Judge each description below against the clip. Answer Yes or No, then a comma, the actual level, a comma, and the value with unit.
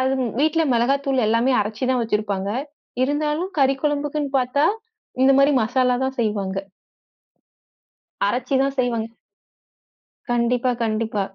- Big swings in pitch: No, average, 3.5 semitones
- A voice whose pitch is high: Yes, very high, 255 Hz